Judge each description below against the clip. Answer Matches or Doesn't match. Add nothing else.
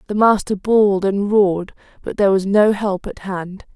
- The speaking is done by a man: Doesn't match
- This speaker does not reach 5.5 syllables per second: Matches